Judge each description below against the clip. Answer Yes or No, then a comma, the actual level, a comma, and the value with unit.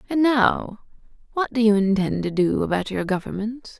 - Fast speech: No, average, 175 wpm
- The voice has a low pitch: No, high, 220 Hz